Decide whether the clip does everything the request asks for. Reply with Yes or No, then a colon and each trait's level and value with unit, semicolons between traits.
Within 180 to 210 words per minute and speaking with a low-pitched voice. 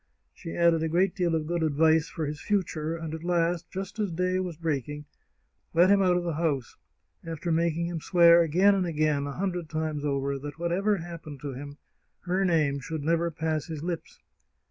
No: average, 195 wpm; medium, 165 Hz